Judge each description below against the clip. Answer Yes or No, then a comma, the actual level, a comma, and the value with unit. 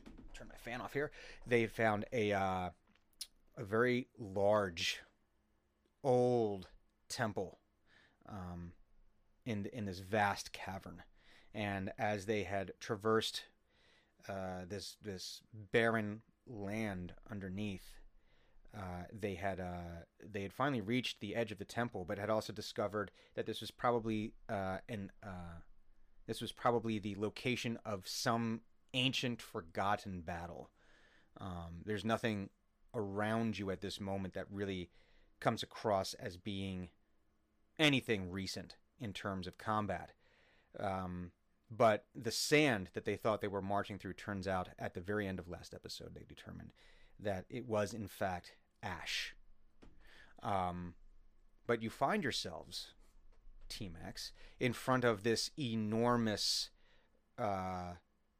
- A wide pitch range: No, average, 2.9 semitones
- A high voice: No, low, 105 Hz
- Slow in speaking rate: Yes, slow, 130 wpm